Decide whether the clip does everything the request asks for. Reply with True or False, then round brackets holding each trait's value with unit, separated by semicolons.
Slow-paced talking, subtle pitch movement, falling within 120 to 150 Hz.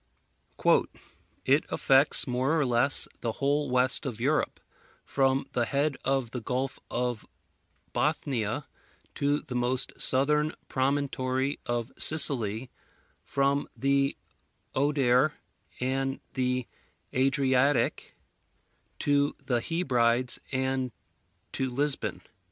True (100 wpm; 2.1 semitones; 135 Hz)